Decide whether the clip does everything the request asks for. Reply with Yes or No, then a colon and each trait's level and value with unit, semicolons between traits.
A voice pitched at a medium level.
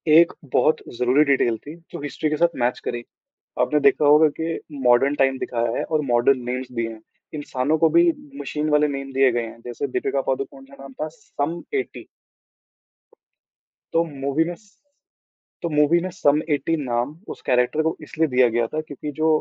Yes: medium, 145 Hz